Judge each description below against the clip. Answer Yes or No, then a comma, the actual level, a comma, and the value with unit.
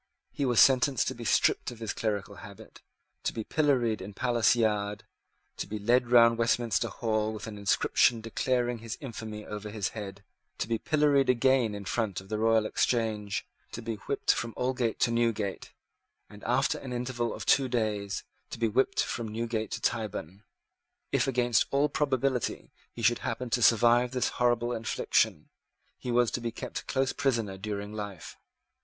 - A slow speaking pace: No, average, 175 wpm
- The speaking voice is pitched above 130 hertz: No, low, 115 Hz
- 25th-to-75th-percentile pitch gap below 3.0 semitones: Yes, narrow, 2.5 semitones